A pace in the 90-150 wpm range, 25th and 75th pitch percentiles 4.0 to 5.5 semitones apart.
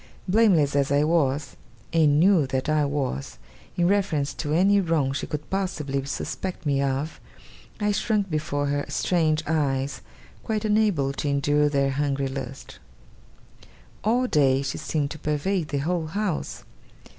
Yes: average, 145 wpm; average, 4.3 semitones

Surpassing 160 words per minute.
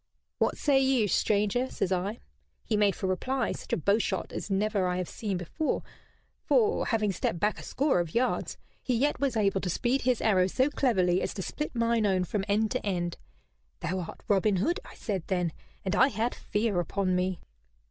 Yes: average, 200 wpm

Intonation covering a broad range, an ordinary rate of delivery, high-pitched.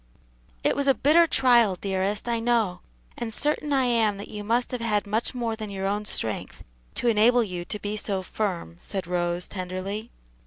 No: average, 3.8 semitones; average, 190 wpm; high, 210 Hz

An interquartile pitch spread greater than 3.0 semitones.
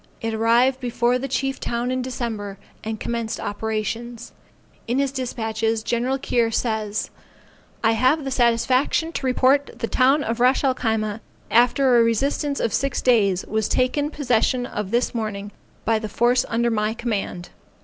No: narrow, 2.5 semitones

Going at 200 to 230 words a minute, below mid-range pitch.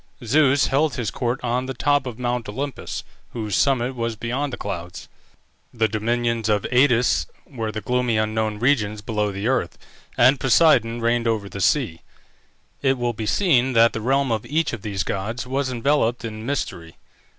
No: average, 175 wpm; low, 120 Hz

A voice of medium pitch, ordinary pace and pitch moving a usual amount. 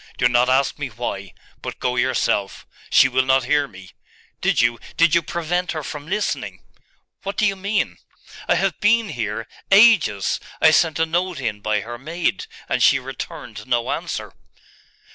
No: medium, 145 Hz; average, 170 wpm; wide, 6.9 semitones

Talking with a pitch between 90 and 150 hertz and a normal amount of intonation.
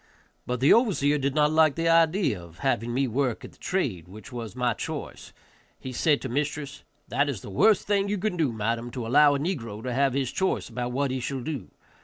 Yes: low, 135 Hz; average, 4.6 semitones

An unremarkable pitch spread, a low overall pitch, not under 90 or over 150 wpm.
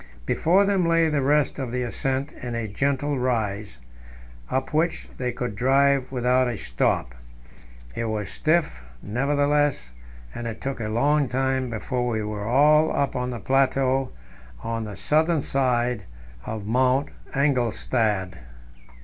Yes: average, 3.6 semitones; low, 130 Hz; average, 140 wpm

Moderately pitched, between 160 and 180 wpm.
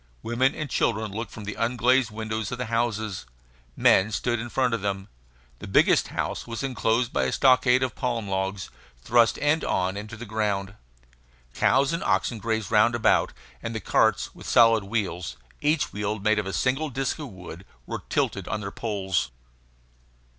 No: low, 110 Hz; average, 175 wpm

